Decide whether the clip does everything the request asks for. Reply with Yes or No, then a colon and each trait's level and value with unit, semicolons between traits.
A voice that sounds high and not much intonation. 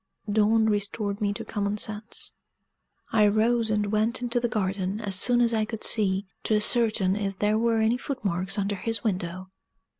Yes: high, 210 Hz; narrow, 2.1 semitones